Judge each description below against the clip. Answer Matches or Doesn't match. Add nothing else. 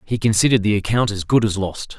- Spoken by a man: Matches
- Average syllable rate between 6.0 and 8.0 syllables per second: Matches